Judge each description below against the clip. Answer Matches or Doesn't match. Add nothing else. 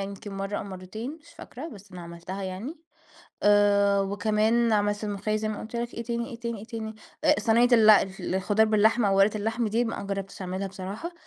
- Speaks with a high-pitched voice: Matches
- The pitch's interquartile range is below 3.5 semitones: Matches